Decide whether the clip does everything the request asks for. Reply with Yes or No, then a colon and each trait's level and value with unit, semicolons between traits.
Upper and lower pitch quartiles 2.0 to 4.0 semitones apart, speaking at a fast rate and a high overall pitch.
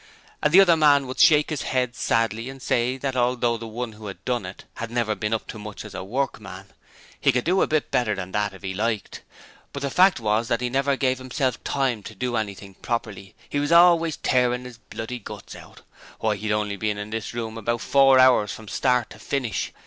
No: average, 3.7 semitones; fast, 230 wpm; low, 120 Hz